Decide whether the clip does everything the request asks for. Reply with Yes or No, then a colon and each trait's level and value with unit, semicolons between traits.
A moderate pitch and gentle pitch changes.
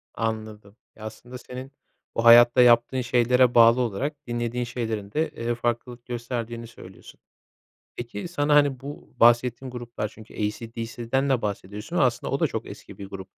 No: low, 120 Hz; narrow, 1.8 semitones